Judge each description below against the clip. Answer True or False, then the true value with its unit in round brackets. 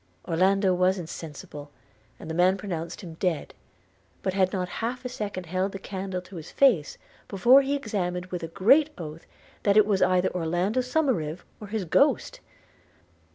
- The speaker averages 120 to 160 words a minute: False (175 wpm)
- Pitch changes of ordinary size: True (3.5 semitones)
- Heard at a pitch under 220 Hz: True (185 Hz)